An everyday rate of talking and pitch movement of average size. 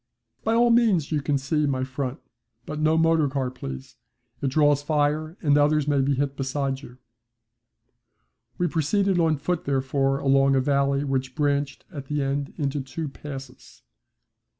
No: average, 155 wpm; narrow, 2.1 semitones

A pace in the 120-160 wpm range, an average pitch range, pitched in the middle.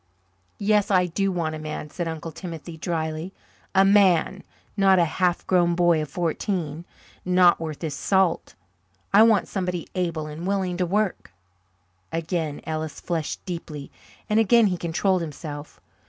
Yes: average, 150 wpm; average, 3.2 semitones; medium, 175 Hz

